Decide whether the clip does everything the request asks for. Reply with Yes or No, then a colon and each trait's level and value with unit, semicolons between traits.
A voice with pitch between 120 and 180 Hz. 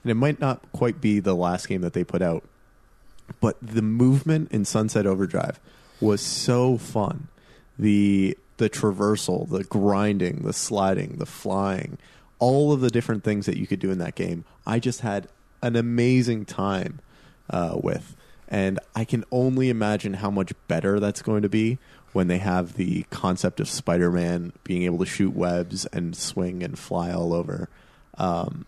No: low, 105 Hz